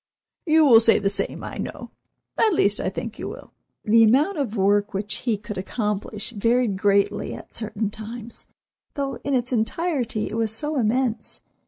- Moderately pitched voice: No, high, 225 Hz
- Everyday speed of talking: Yes, average, 170 wpm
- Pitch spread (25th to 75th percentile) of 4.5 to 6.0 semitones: No, average, 3.4 semitones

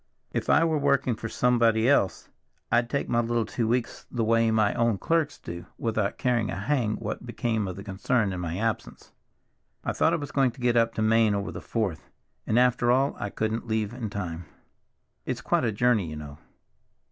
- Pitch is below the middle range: Yes, low, 115 Hz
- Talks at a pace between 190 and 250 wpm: Yes, fast, 205 wpm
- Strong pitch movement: No, average, 3.0 semitones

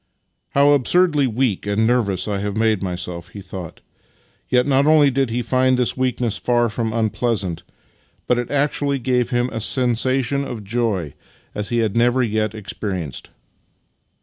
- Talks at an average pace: Yes, average, 165 wpm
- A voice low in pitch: Yes, low, 120 Hz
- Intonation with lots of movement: No, average, 3.9 semitones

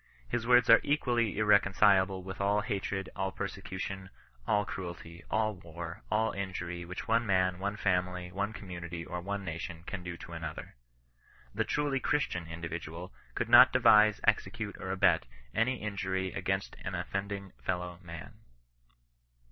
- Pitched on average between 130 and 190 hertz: No, very low, 95 Hz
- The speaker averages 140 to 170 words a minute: Yes, average, 150 wpm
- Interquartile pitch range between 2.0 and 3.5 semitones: Yes, average, 2.8 semitones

